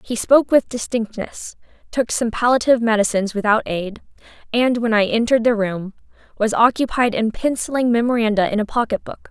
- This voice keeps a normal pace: Yes, average, 150 wpm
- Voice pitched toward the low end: No, high, 225 Hz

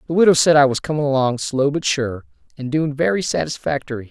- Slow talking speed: No, fast, 205 wpm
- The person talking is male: Yes, male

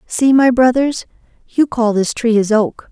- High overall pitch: Yes, high, 240 Hz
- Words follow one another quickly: No, average, 185 wpm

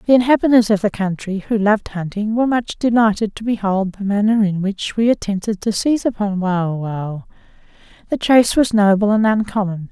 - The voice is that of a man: No, female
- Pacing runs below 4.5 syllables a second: No, 5.5 syllables/s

